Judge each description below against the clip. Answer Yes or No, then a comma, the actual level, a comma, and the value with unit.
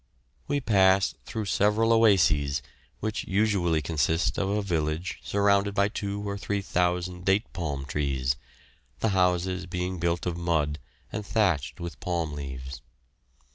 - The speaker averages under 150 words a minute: Yes, slow, 135 wpm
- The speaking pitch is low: Yes, very low, 90 Hz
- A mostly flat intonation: No, average, 4.1 semitones